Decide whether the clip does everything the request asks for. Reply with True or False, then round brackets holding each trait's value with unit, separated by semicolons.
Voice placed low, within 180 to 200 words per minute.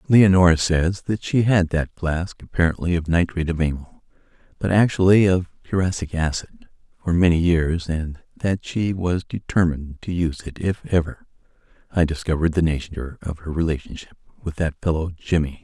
False (85 Hz; 155 wpm)